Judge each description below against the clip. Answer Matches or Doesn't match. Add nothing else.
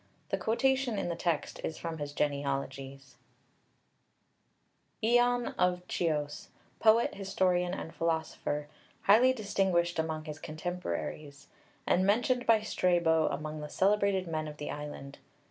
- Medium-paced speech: Doesn't match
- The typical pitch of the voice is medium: Matches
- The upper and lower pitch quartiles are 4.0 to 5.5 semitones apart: Matches